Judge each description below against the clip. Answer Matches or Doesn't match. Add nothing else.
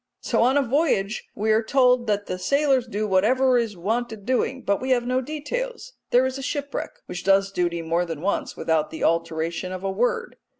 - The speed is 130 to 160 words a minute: Doesn't match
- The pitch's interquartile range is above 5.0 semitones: Matches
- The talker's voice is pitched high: Matches